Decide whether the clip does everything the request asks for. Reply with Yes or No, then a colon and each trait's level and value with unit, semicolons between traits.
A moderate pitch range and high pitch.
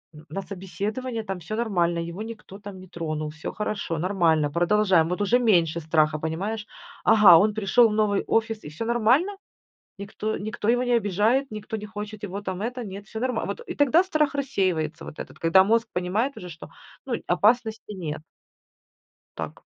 Yes: average, 4.2 semitones; high, 205 Hz